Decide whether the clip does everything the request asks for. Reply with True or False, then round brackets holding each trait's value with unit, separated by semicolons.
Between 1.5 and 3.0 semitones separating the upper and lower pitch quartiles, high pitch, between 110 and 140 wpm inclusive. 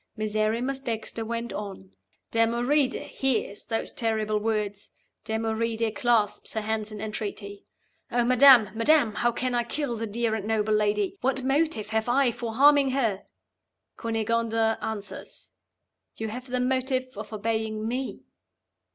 True (2.6 semitones; 225 Hz; 135 wpm)